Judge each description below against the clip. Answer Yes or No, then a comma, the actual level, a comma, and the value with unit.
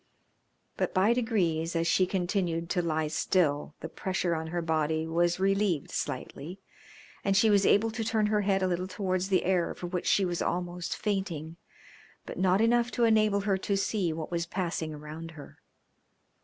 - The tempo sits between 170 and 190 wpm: Yes, average, 180 wpm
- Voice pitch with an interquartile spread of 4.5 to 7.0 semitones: No, average, 3.2 semitones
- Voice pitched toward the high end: No, medium, 180 Hz